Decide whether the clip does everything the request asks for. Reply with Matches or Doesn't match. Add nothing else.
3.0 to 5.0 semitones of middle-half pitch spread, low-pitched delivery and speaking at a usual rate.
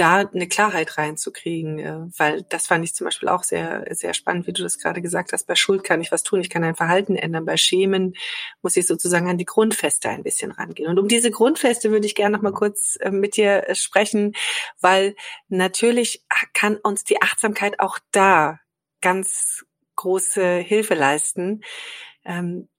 Doesn't match